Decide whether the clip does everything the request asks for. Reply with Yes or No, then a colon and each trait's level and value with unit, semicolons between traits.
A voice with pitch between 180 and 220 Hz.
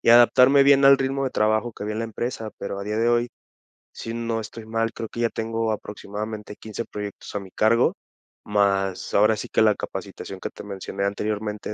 No: low, 110 Hz